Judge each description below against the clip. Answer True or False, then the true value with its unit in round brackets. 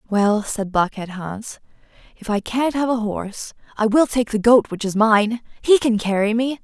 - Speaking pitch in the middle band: False (225 Hz)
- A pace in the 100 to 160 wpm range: False (200 wpm)